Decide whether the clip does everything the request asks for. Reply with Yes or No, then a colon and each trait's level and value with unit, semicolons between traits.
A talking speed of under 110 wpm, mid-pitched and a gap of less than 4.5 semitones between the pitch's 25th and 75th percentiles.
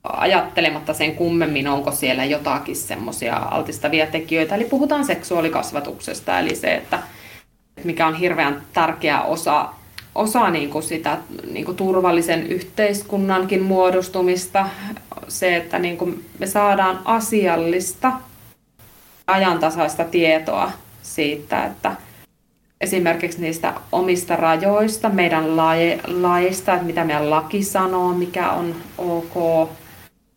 Yes: average, 100 wpm; medium, 175 Hz; narrow, 2.6 semitones